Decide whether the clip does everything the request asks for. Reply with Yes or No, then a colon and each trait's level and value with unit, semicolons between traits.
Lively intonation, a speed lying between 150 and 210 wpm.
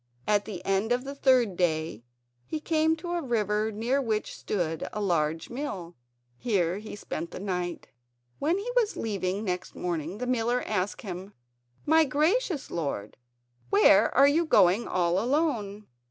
Yes: wide, 7.2 semitones; average, 155 wpm